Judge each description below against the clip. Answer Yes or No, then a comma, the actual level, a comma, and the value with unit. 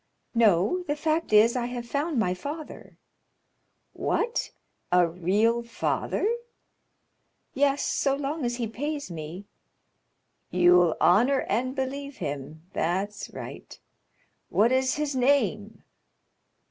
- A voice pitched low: No, high, 235 Hz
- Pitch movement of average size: No, wide, 7.3 semitones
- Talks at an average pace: No, slow, 110 wpm